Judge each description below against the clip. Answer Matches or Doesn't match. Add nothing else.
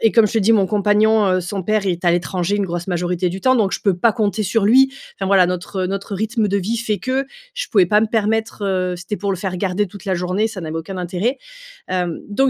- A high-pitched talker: Matches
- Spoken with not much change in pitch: Doesn't match